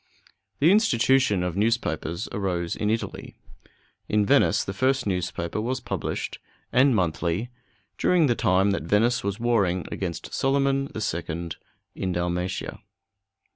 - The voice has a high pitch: No, low, 100 Hz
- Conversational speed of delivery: No, slow, 130 wpm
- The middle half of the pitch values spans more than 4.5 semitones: Yes, wide, 5.5 semitones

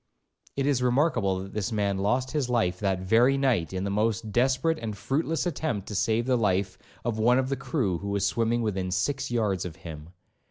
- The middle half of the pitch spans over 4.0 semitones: Yes, average, 5.0 semitones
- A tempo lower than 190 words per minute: No, fast, 205 wpm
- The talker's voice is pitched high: No, low, 110 Hz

